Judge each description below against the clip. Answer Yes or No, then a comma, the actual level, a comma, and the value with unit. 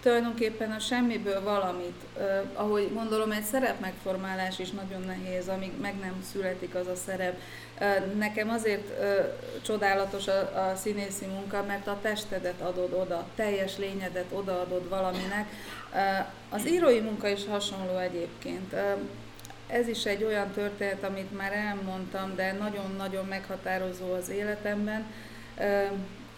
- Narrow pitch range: Yes, narrow, 1.8 semitones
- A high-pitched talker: Yes, high, 195 Hz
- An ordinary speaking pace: Yes, average, 135 wpm